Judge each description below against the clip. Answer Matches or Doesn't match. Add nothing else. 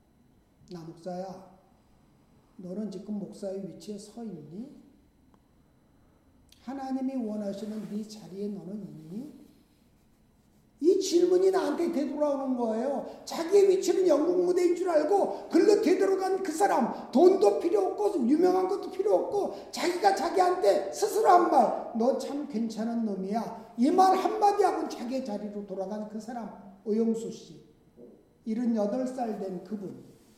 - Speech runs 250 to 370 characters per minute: Matches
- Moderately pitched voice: Doesn't match